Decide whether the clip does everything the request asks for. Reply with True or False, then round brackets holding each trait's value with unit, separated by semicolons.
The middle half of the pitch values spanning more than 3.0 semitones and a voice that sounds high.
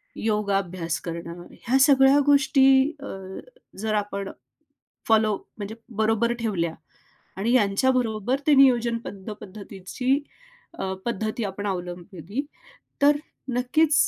True (4.6 semitones; 215 Hz)